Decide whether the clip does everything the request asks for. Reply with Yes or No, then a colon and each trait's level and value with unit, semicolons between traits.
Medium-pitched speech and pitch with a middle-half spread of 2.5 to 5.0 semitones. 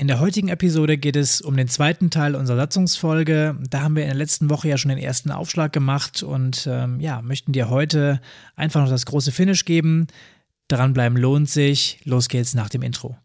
Yes: medium, 145 Hz; average, 2.9 semitones